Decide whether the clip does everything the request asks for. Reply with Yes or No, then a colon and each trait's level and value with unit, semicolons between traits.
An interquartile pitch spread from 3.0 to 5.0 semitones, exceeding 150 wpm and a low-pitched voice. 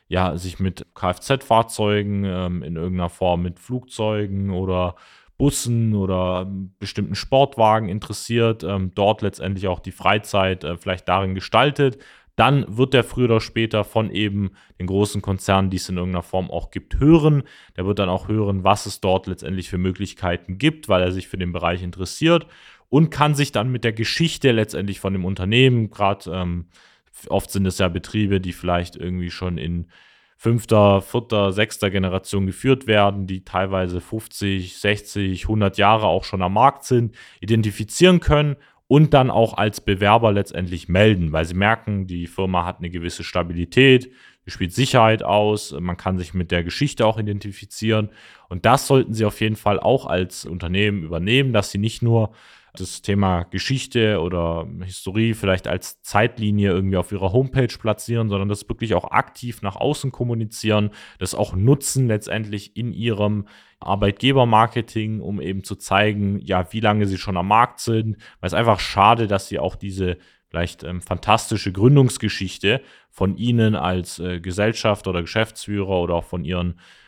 Yes: average, 3.4 semitones; average, 160 wpm; low, 100 Hz